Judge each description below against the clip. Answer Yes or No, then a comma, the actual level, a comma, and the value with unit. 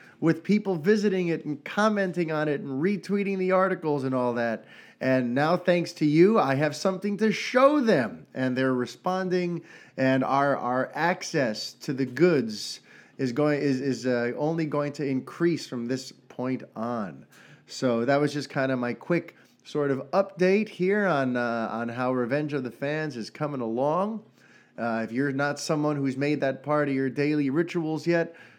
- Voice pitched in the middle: Yes, medium, 145 Hz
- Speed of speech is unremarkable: Yes, average, 180 wpm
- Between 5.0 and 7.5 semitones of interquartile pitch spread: Yes, average, 5.3 semitones